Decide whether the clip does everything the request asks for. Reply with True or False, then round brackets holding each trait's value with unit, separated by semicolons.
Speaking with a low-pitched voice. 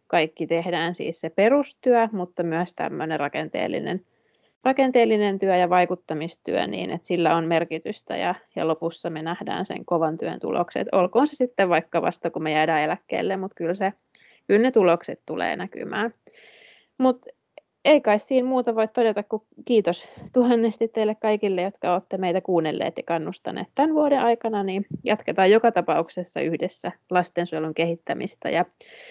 False (190 Hz)